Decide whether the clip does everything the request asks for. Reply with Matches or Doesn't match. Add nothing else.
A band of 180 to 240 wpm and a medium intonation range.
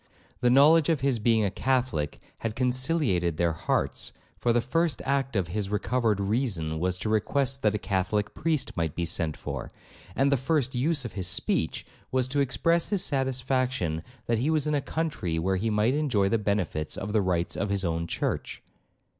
Doesn't match